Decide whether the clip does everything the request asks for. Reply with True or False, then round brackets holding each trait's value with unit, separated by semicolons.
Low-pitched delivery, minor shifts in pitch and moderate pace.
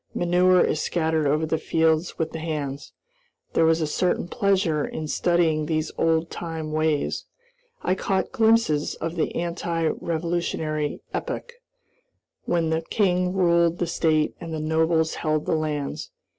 False (160 Hz; 1.8 semitones; 145 wpm)